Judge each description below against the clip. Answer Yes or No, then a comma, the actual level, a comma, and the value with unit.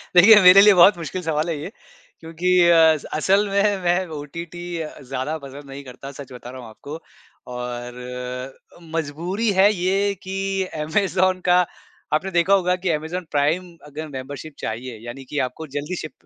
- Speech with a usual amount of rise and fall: Yes, average, 5.0 semitones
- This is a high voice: No, medium, 160 Hz